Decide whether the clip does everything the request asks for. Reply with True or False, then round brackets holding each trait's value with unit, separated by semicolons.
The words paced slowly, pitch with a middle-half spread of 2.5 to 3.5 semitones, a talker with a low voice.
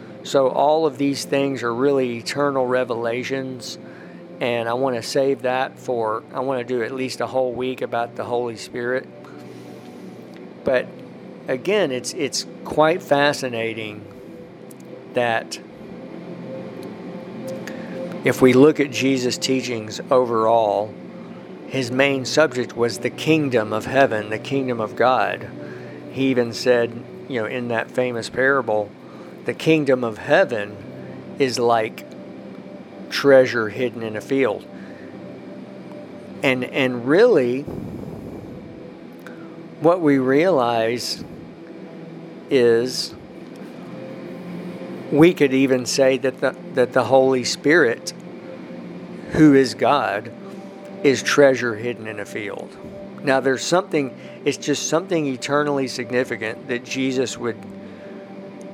True (115 wpm; 2.8 semitones; 125 Hz)